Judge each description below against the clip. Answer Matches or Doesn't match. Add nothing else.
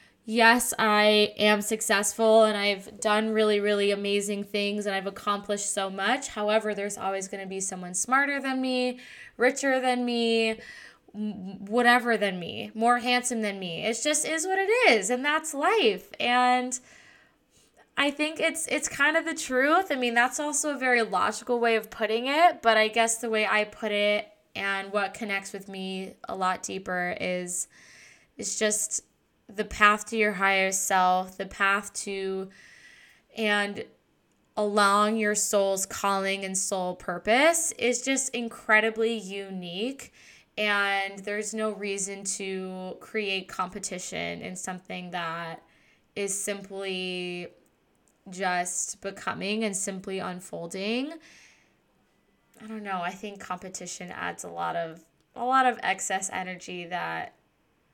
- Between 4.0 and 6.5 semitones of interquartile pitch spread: Doesn't match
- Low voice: Doesn't match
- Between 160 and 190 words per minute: Doesn't match